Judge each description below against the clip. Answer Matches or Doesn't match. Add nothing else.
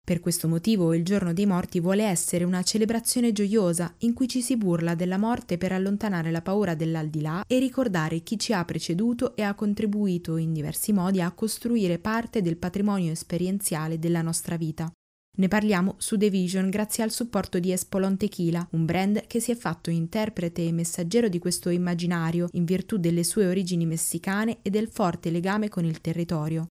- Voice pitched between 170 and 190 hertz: Matches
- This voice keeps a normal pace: Doesn't match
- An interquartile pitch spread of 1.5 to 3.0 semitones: Doesn't match